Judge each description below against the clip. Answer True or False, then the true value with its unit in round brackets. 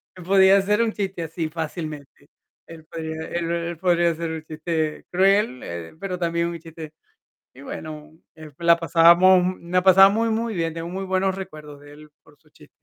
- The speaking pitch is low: False (170 Hz)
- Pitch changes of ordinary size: True (3.0 semitones)